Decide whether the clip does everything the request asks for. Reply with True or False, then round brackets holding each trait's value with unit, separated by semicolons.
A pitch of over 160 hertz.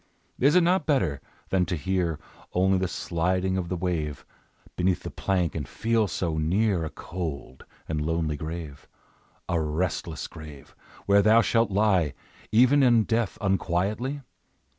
False (90 Hz)